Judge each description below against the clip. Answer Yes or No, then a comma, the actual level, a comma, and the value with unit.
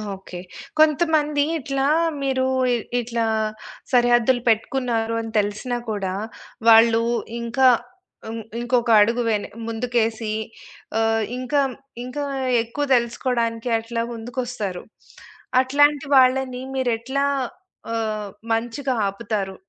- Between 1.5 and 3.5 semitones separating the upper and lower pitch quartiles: Yes, narrow, 2.6 semitones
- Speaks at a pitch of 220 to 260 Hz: Yes, high, 240 Hz